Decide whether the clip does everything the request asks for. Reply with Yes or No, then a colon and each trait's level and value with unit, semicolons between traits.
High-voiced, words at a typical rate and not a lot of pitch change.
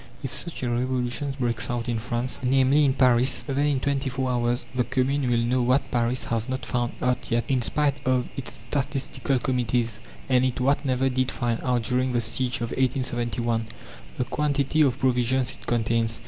No: low, 125 Hz; average, 190 wpm; narrow, 1.8 semitones